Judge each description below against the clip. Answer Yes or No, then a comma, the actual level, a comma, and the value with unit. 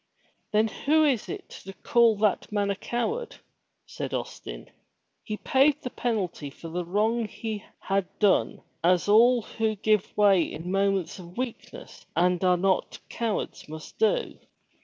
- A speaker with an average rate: Yes, average, 145 wpm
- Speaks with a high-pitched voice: Yes, high, 210 Hz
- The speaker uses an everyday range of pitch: Yes, average, 4.2 semitones